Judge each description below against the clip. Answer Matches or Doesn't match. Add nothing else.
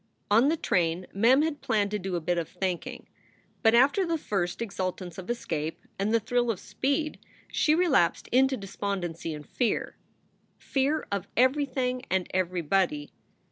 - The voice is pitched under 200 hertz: Doesn't match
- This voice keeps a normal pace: Matches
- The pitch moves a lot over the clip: Matches